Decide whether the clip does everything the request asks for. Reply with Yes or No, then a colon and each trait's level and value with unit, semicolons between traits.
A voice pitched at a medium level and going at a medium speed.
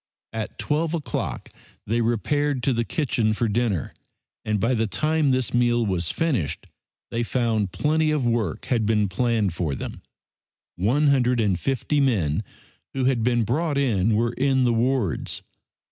No: low, 120 Hz; average, 160 wpm